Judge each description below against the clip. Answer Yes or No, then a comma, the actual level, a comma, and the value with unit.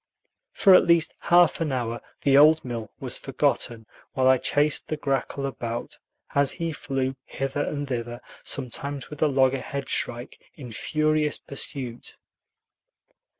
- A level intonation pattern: No, average, 3.0 semitones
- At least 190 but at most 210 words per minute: No, average, 140 wpm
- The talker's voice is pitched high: No, medium, 140 Hz